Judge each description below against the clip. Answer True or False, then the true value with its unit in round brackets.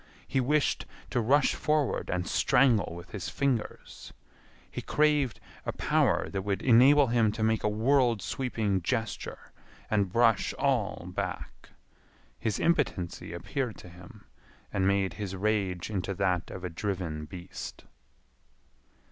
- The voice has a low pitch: True (105 Hz)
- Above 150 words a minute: False (135 wpm)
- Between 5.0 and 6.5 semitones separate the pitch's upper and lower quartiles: True (5.3 semitones)